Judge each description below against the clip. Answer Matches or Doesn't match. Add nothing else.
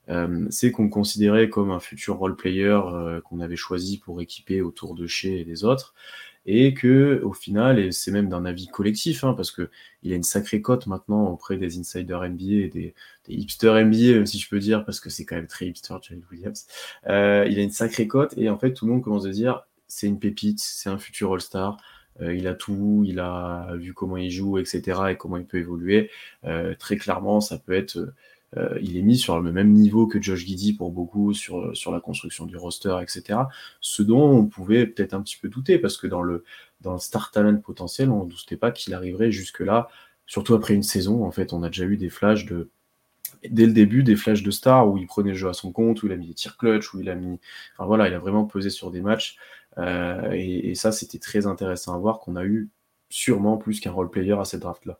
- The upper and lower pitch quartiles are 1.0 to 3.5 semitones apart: Matches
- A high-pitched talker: Doesn't match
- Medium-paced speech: Doesn't match